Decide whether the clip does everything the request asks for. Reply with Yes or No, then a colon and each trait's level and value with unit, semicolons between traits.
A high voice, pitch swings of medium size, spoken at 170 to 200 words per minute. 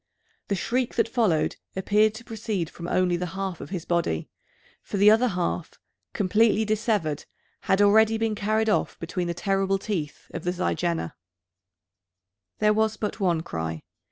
No: high, 195 Hz; average, 3.8 semitones; average, 155 wpm